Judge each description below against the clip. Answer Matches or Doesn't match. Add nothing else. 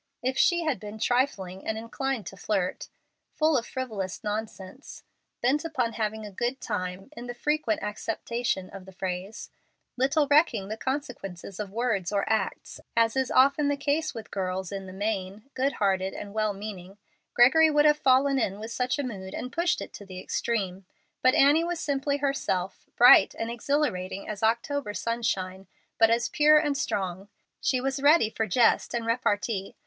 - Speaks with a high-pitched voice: Matches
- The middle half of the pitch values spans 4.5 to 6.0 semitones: Matches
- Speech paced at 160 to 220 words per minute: Matches